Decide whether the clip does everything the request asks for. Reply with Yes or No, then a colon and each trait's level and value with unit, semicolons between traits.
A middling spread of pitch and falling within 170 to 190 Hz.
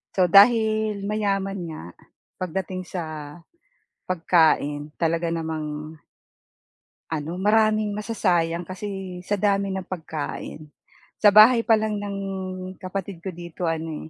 Yes: average, 4.0 semitones; medium, 185 Hz